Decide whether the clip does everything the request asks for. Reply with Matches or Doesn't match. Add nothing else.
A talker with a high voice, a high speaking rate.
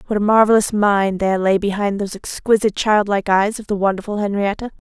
Doesn't match